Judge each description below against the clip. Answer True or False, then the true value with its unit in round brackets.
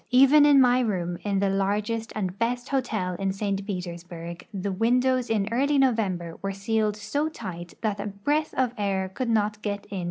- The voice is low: False (210 Hz)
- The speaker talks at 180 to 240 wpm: True (185 wpm)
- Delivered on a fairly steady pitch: False (4.2 semitones)